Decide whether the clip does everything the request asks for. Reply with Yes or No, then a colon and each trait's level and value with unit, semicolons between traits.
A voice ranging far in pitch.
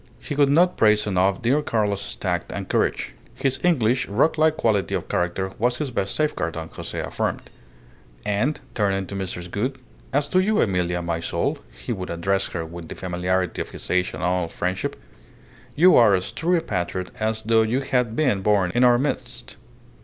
Yes: wide, 6.2 semitones